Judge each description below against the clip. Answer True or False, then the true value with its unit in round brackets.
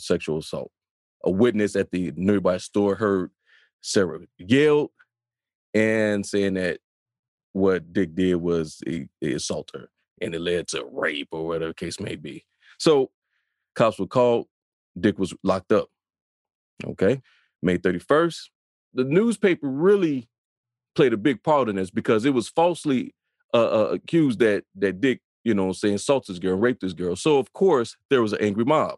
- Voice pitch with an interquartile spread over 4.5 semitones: True (5.2 semitones)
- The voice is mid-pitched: False (105 Hz)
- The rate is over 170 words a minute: False (165 wpm)